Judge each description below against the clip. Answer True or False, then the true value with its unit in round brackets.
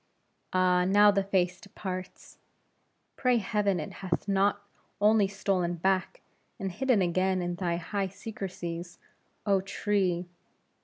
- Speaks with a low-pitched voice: False (190 Hz)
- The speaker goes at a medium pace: False (120 wpm)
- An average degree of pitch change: False (2.0 semitones)